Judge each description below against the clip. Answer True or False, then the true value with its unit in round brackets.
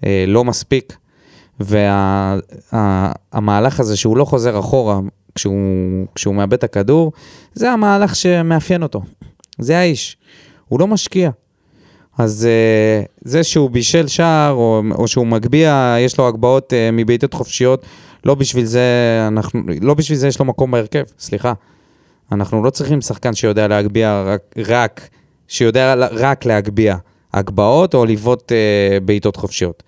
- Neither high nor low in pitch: False (120 Hz)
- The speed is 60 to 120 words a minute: False (135 wpm)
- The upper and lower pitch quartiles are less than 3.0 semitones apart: False (4.8 semitones)